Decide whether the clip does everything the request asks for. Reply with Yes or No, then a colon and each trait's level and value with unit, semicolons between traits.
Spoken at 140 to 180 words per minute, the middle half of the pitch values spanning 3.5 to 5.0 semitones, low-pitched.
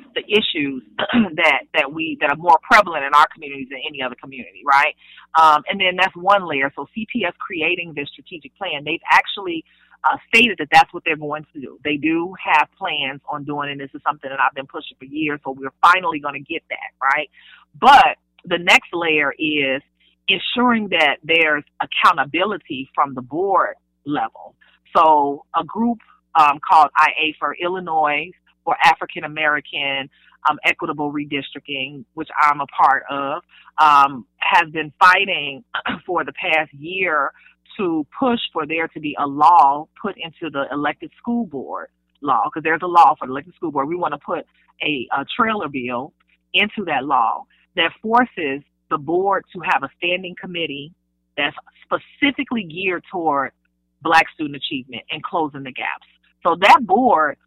No: average, 170 wpm; average, 4.7 semitones; medium, 160 Hz